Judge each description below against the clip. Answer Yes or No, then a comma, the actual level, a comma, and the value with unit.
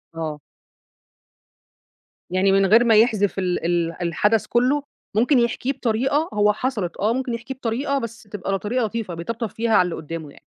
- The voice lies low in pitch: No, high, 220 Hz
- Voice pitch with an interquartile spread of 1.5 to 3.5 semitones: No, average, 4.6 semitones